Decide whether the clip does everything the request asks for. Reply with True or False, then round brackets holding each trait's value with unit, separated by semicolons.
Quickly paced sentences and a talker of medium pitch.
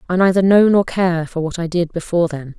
True (255 wpm; 175 Hz)